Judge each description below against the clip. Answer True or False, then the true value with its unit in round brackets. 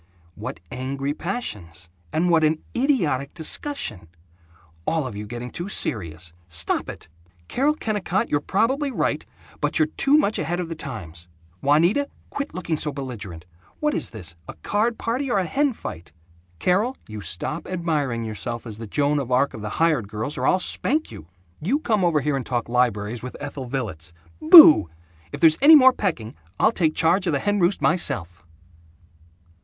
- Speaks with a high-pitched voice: False (150 Hz)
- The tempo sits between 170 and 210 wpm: True (175 wpm)